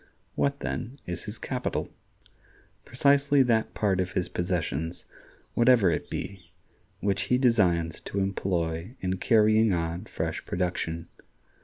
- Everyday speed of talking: No, slow, 125 wpm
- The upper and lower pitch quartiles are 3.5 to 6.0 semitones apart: Yes, average, 5.3 semitones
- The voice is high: No, very low, 95 Hz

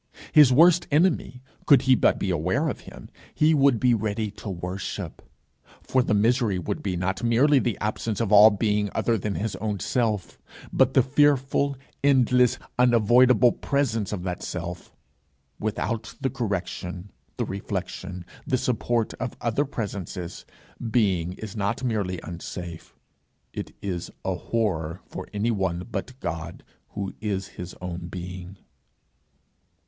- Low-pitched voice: Yes, low, 105 Hz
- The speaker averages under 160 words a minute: Yes, average, 140 wpm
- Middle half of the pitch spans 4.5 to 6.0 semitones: Yes, average, 5.2 semitones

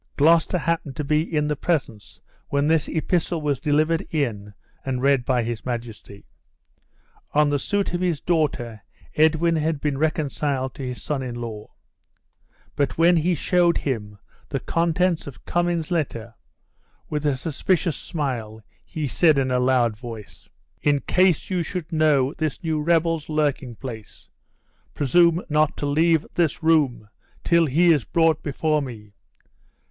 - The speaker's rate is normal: Yes, average, 150 wpm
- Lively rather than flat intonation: No, average, 4.2 semitones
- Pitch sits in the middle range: Yes, medium, 150 Hz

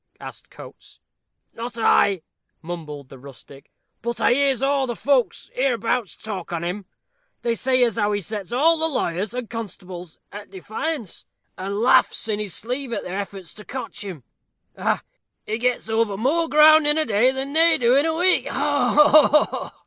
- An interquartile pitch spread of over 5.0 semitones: Yes, wide, 5.5 semitones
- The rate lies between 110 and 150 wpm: No, average, 180 wpm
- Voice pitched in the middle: No, high, 230 Hz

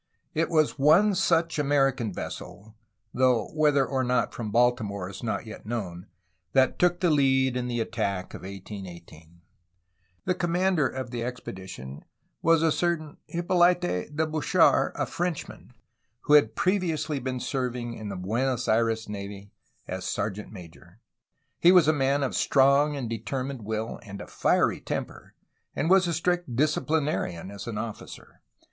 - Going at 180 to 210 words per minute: No, average, 155 wpm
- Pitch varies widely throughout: Yes, wide, 6.5 semitones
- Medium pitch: No, low, 130 Hz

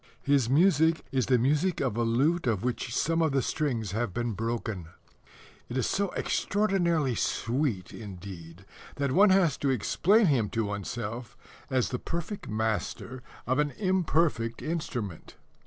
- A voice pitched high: No, low, 130 Hz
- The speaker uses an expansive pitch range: Yes, wide, 6.2 semitones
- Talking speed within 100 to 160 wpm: Yes, average, 150 wpm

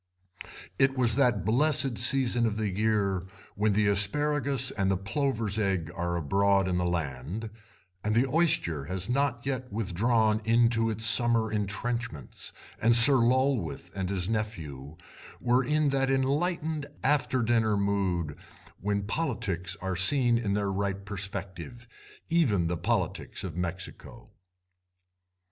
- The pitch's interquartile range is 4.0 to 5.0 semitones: Yes, average, 4.7 semitones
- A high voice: No, low, 110 Hz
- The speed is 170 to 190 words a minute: No, slow, 135 wpm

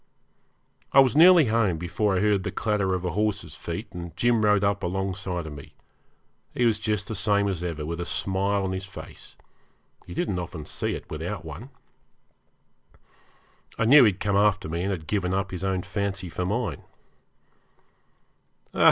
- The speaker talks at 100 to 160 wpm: No, average, 180 wpm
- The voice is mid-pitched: No, very low, 95 Hz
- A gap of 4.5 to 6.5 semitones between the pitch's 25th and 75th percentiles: No, average, 2.8 semitones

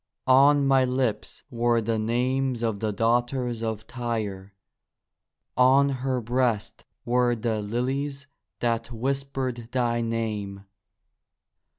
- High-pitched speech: No, low, 120 Hz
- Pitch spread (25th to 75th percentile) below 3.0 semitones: Yes, narrow, 2.4 semitones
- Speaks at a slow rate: Yes, slow, 105 wpm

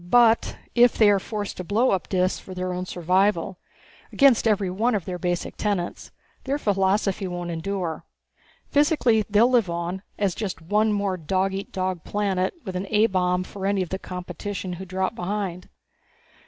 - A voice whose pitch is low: No, high, 190 Hz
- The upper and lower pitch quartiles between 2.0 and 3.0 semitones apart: Yes, narrow, 2.5 semitones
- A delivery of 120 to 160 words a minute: No, average, 175 wpm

